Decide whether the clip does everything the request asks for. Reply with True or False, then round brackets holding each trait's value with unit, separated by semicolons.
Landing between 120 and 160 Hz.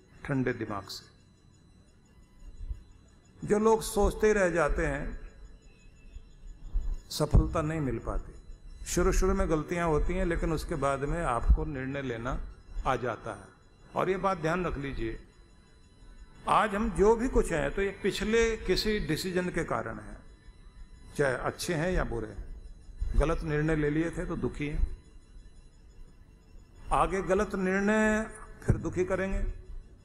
True (135 Hz)